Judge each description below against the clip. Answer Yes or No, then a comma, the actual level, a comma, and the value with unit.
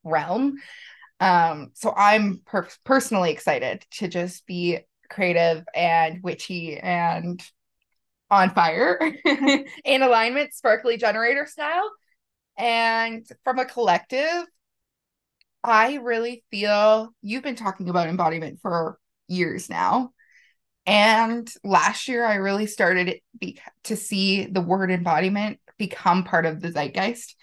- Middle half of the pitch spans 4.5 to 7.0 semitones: Yes, average, 5.1 semitones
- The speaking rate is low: Yes, slow, 115 wpm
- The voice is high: Yes, high, 205 Hz